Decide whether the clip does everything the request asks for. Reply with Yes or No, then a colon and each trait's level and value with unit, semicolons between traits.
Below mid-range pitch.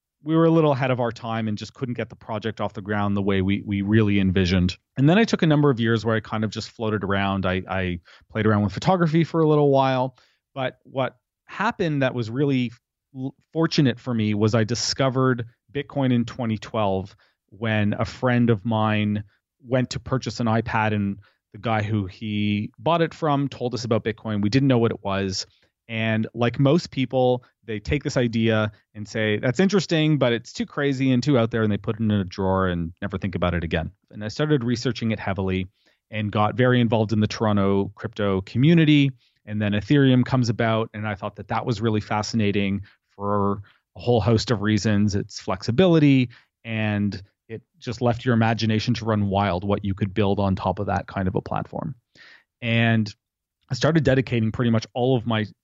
Yes: low, 110 Hz